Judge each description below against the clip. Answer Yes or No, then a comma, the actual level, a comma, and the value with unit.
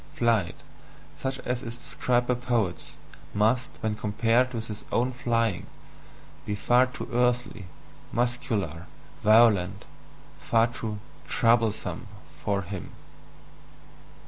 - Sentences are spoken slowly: Yes, slow, 105 wpm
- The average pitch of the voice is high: No, low, 115 Hz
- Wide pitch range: No, average, 2.8 semitones